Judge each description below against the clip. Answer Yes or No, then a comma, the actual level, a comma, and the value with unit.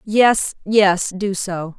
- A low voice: No, high, 195 Hz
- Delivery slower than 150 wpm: Yes, slow, 135 wpm